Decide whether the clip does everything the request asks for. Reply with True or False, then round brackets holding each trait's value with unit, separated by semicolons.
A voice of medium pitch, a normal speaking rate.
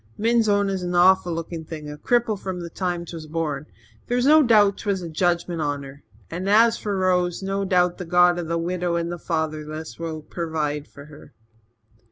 True (175 Hz; 190 wpm)